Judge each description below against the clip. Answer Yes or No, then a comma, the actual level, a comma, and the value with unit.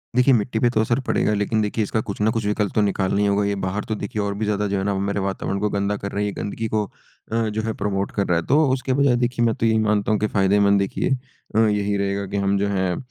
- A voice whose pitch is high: No, low, 105 Hz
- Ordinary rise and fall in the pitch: No, narrow, 1.8 semitones